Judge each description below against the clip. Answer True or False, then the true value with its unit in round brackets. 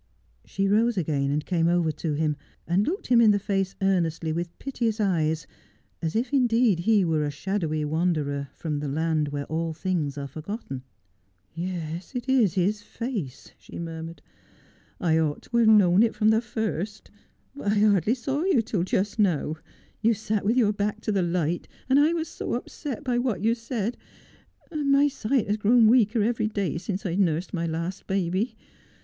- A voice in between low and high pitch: False (195 Hz)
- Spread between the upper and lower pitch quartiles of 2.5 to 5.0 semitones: False (5.6 semitones)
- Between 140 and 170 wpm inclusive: False (190 wpm)